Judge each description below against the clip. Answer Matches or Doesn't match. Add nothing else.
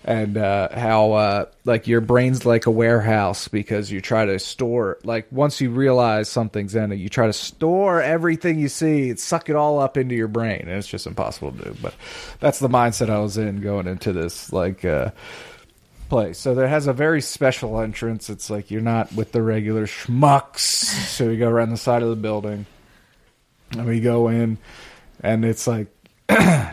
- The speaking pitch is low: Matches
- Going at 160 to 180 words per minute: Doesn't match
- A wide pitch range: Doesn't match